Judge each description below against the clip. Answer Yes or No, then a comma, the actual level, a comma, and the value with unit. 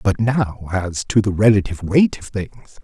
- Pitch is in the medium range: No, low, 100 Hz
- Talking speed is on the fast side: No, average, 190 wpm